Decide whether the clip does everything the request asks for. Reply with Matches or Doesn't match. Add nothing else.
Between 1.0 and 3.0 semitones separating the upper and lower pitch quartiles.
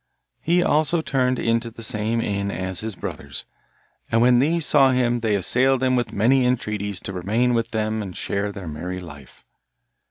Doesn't match